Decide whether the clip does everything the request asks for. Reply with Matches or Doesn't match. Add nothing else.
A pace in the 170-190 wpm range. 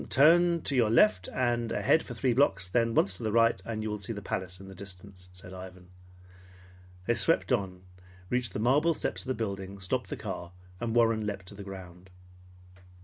Doesn't match